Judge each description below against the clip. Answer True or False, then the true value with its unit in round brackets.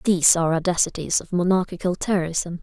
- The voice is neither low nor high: True (175 Hz)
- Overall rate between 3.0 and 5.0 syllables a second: False (6.2 syllables/s)